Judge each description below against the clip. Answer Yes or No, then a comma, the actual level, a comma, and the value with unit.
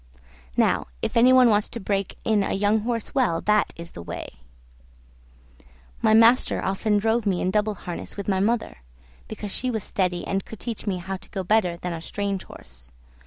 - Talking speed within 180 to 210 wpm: Yes, average, 195 wpm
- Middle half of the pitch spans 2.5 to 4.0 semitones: Yes, average, 3.1 semitones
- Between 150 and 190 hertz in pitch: No, high, 205 Hz